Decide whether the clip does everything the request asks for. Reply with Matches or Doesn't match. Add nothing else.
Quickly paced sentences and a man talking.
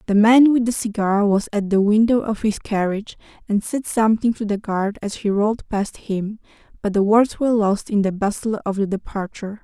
Doesn't match